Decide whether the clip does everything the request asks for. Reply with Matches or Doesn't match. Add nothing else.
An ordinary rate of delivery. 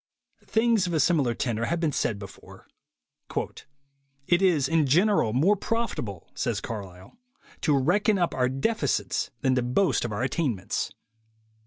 Matches